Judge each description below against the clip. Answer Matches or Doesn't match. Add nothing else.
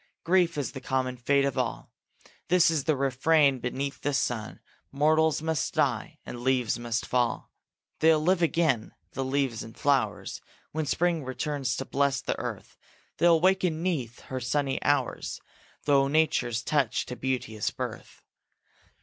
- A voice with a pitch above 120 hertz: Matches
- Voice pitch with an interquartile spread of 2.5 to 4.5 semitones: Matches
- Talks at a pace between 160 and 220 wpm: Doesn't match